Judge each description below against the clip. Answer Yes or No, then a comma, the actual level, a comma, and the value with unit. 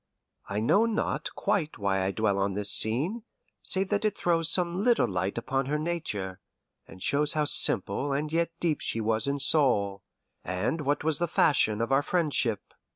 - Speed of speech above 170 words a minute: Yes, average, 180 wpm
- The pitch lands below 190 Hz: Yes, medium, 140 Hz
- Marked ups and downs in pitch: Yes, wide, 8.1 semitones